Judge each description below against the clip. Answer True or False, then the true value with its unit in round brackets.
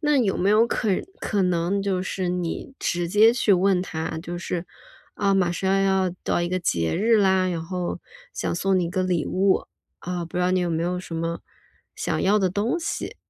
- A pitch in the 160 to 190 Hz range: True (185 Hz)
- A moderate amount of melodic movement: False (2.2 semitones)